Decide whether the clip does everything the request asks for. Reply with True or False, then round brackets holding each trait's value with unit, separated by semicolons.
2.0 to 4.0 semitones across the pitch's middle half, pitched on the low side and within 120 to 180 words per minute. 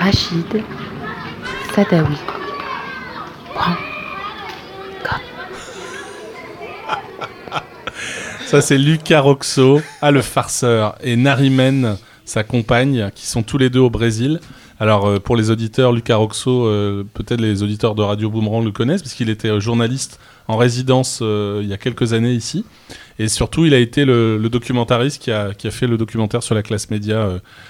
True (3.7 semitones; 120 Hz; 150 wpm)